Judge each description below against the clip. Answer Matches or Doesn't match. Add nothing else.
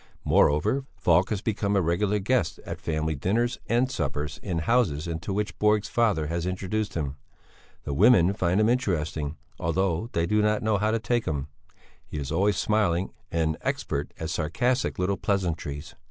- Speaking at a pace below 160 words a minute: Doesn't match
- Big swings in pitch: Doesn't match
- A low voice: Matches